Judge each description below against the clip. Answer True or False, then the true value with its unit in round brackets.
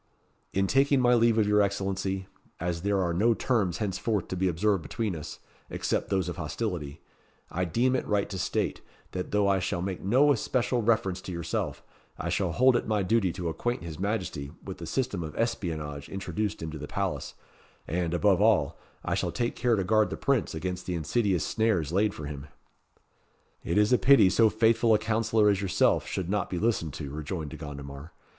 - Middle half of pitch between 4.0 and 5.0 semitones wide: True (4.6 semitones)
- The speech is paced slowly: False (195 wpm)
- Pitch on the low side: True (95 Hz)